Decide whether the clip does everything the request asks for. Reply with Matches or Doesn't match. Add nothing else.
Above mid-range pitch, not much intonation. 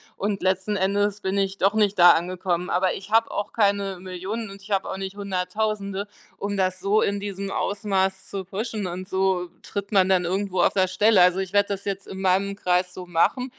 Matches